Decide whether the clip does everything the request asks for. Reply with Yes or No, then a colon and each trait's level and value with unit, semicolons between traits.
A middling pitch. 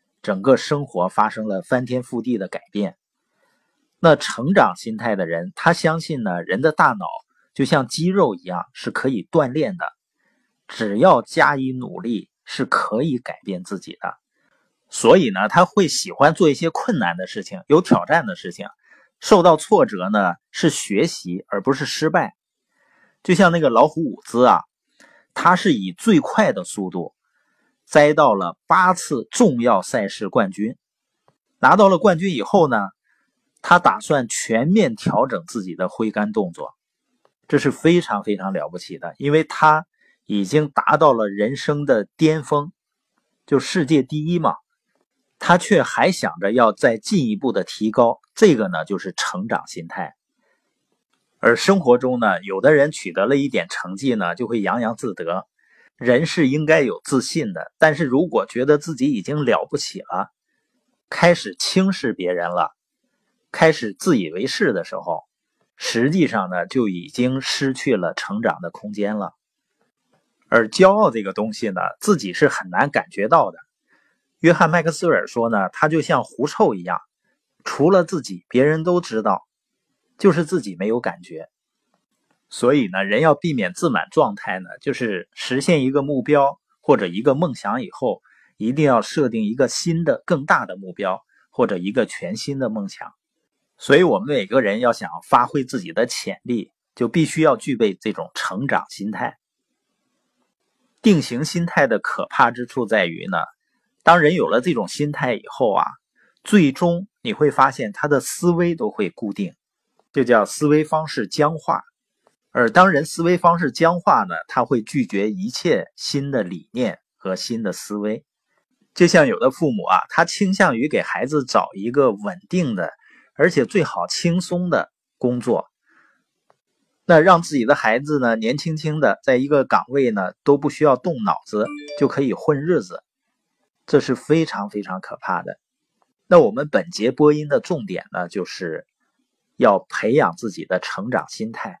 Yes: medium, 150 Hz